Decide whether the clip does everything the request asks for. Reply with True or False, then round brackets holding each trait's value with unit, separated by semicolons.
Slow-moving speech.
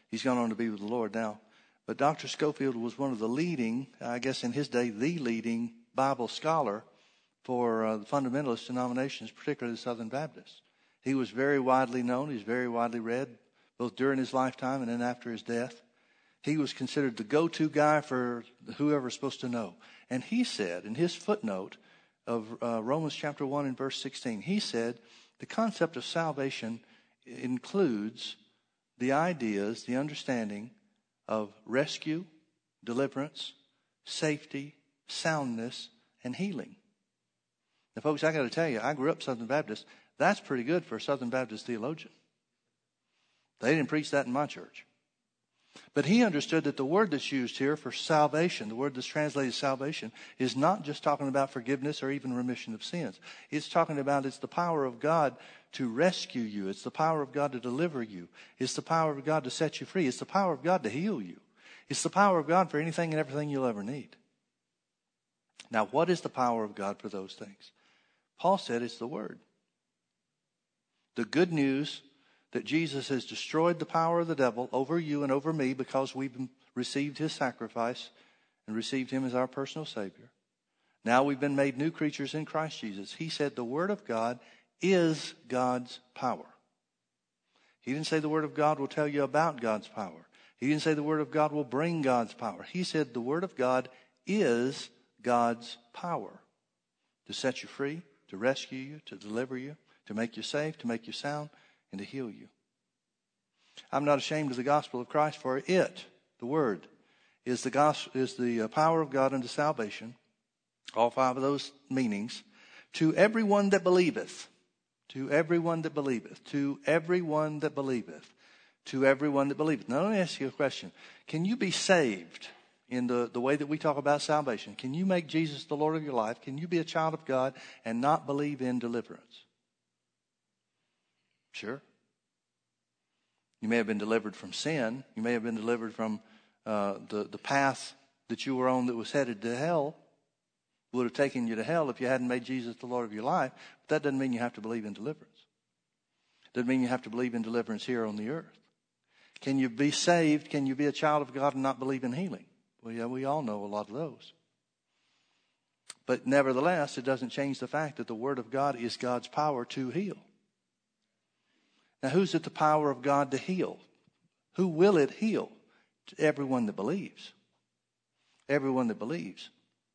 False (185 wpm)